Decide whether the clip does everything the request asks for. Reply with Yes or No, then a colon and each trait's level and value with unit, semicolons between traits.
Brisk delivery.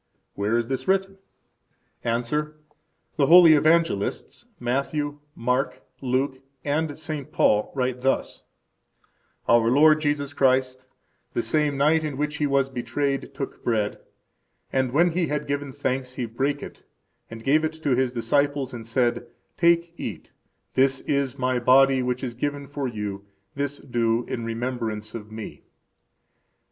No: average, 145 wpm